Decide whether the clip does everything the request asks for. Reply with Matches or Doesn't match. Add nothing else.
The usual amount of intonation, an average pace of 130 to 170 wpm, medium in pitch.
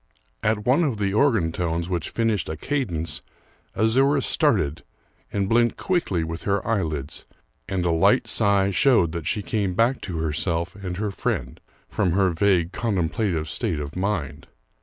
Doesn't match